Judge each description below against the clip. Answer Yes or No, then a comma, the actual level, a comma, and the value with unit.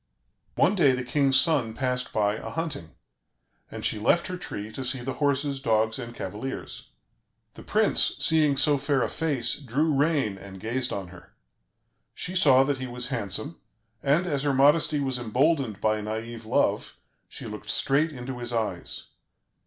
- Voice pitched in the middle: No, low, 130 Hz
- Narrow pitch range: No, average, 4.2 semitones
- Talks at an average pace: Yes, average, 170 wpm